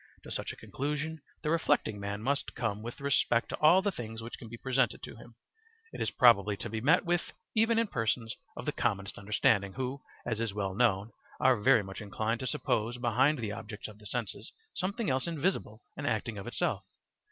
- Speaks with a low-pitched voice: Yes, low, 120 Hz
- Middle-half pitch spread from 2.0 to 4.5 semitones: No, average, 4.9 semitones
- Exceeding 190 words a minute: Yes, fast, 205 wpm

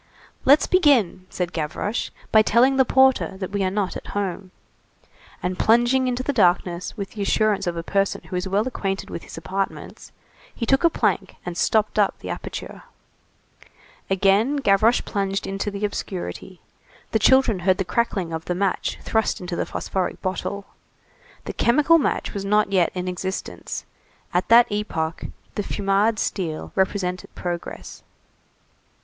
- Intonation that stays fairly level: No, average, 3.5 semitones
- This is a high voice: Yes, high, 195 Hz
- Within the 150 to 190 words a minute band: Yes, average, 155 wpm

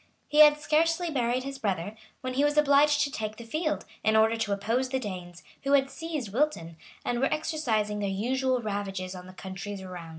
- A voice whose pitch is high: Yes, high, 240 Hz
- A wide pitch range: Yes, wide, 6.3 semitones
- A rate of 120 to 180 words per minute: No, average, 200 wpm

